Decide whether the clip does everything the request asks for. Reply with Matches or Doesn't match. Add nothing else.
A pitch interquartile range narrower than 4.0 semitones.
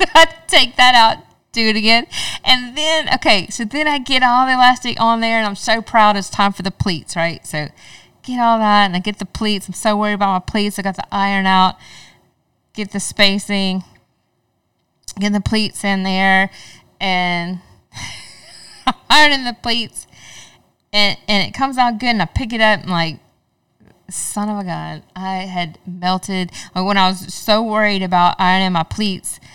Matches